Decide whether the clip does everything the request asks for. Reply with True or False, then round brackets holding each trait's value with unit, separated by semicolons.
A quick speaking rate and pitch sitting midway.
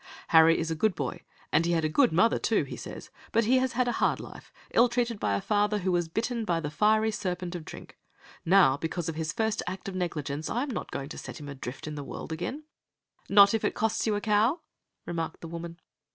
True (240 wpm; 180 Hz)